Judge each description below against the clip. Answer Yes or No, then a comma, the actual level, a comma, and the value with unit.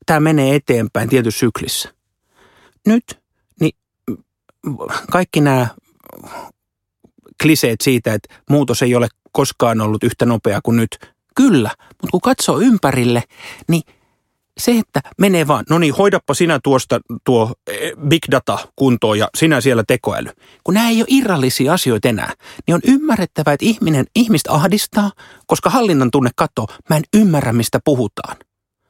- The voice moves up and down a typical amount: No, wide, 7.1 semitones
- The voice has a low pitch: No, medium, 145 Hz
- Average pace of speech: Yes, average, 140 wpm